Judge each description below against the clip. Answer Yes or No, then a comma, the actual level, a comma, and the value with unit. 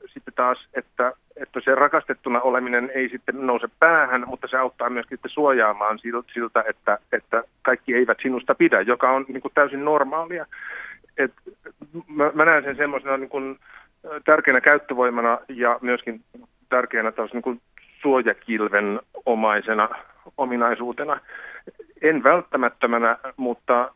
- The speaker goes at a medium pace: Yes, average, 130 wpm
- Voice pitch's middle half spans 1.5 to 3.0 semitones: No, average, 3.6 semitones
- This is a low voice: Yes, low, 130 Hz